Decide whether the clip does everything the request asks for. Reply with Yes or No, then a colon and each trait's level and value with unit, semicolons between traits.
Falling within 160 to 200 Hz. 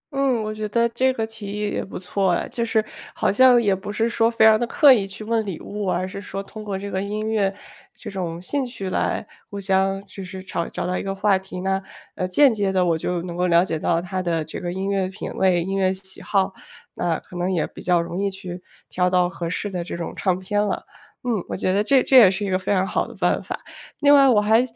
Yes: high, 195 Hz